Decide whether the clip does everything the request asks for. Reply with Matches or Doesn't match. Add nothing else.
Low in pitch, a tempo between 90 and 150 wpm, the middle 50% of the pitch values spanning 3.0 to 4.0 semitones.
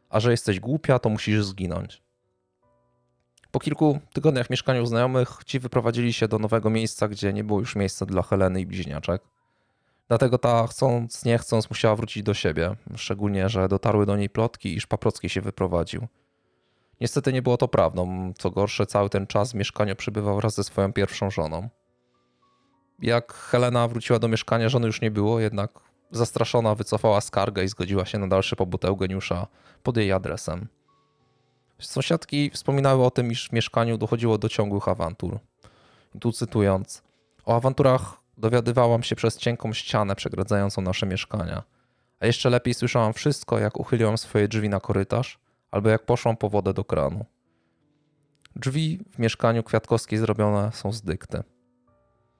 Doesn't match